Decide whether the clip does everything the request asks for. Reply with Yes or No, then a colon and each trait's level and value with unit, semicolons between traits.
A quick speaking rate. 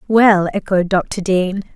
No: slow, 135 wpm